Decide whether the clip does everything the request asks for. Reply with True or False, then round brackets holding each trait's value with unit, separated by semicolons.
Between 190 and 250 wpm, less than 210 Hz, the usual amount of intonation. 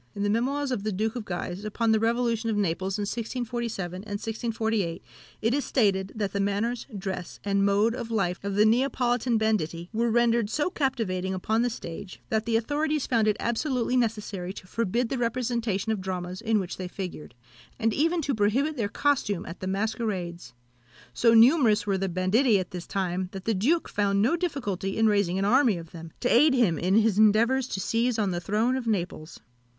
False (195 wpm; 215 Hz; 3.7 semitones)